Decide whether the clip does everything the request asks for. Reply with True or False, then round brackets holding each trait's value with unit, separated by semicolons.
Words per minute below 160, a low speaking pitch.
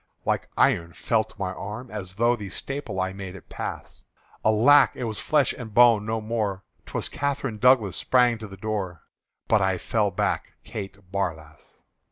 False (175 wpm; 105 Hz)